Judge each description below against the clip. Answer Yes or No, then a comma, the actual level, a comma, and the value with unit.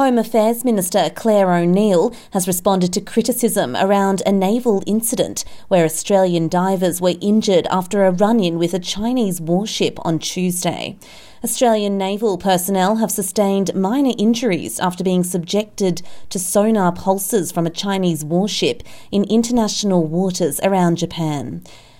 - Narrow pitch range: No, average, 3.1 semitones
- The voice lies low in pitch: No, high, 195 Hz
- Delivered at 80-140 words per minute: Yes, slow, 135 wpm